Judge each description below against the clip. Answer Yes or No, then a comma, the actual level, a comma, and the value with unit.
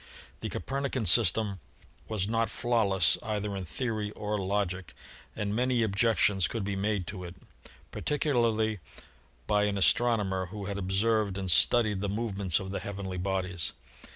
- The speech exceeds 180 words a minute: No, average, 150 wpm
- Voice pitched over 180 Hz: No, low, 100 Hz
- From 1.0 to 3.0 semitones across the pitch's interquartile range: Yes, narrow, 2.6 semitones